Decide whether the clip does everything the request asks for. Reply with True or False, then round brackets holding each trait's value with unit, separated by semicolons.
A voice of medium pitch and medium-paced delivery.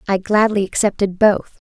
False (200 Hz; 145 wpm)